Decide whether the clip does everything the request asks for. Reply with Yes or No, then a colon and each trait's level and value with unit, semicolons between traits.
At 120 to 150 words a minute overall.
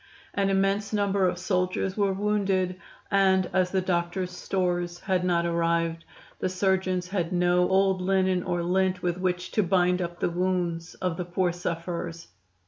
No: average, 160 wpm